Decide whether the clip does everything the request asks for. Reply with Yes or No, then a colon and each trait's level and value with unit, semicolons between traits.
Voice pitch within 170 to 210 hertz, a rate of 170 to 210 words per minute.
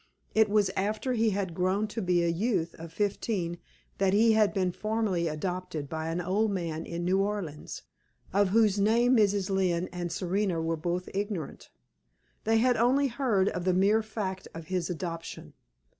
Yes: high, 190 Hz; average, 175 wpm